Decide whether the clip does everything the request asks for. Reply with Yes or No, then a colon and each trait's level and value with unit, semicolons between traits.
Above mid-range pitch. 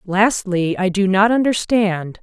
Yes: high, 200 Hz